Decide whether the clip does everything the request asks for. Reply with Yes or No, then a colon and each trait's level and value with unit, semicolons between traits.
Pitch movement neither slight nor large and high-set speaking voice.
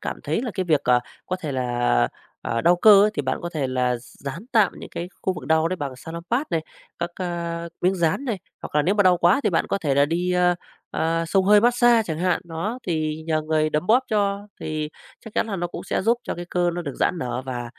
No: average, 3.9 semitones; medium, 170 Hz